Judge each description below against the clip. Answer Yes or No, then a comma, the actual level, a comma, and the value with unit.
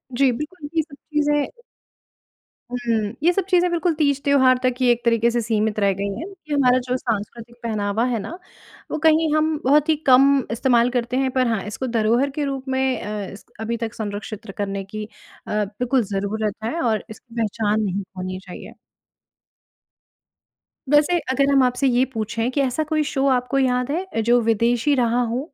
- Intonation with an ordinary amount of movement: Yes, average, 4.3 semitones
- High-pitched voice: Yes, very high, 250 Hz